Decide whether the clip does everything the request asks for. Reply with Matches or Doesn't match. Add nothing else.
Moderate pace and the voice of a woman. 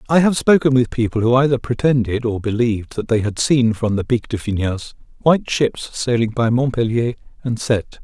Doesn't match